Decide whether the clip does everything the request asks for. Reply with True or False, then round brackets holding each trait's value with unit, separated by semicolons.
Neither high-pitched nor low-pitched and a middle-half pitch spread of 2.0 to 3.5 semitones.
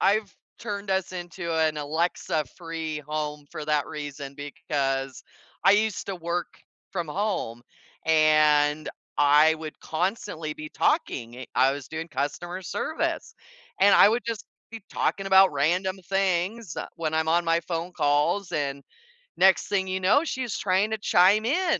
False (165 Hz; 4.5 semitones)